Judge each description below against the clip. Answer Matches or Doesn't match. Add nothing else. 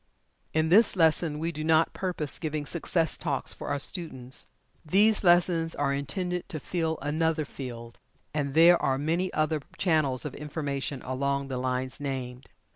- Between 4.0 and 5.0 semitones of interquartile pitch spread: Doesn't match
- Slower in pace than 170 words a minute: Matches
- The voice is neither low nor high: Matches